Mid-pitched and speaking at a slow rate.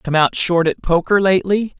No: medium, 180 Hz; average, 200 wpm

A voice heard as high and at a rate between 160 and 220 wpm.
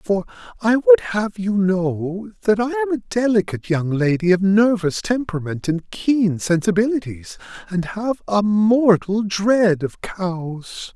No: high, 200 Hz; average, 140 wpm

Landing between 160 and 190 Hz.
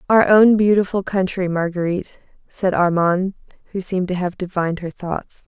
Yes: medium, 185 Hz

